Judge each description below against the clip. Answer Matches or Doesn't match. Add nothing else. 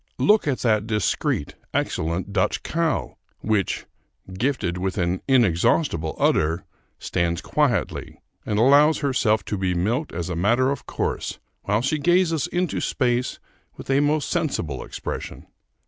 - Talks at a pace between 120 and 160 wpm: Matches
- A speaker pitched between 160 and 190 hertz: Doesn't match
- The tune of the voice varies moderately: Doesn't match